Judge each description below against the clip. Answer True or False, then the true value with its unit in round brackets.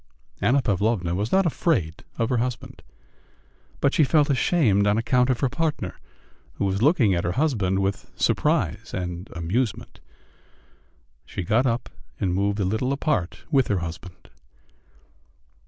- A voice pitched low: True (110 Hz)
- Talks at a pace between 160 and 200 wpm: False (145 wpm)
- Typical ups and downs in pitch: False (5.9 semitones)